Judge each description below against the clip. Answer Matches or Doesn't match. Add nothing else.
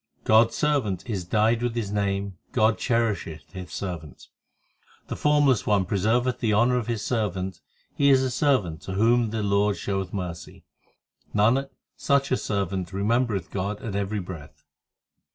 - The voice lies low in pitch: Matches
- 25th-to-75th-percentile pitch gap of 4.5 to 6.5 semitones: Doesn't match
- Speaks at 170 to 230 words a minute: Doesn't match